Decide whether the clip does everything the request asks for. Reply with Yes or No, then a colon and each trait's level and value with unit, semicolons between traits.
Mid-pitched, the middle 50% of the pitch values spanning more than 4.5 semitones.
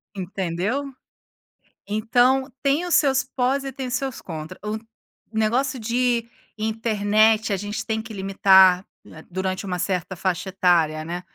No: high, 215 Hz; average, 4.9 semitones